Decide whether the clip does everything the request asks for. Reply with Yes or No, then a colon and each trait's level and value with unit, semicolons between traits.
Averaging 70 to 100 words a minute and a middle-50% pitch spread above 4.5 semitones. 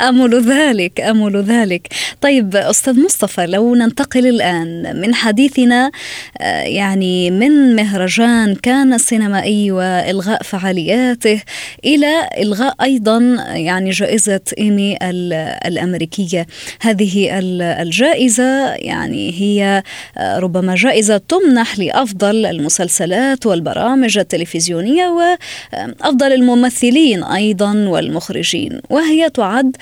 Yes: average, 85 wpm; average, 5.2 semitones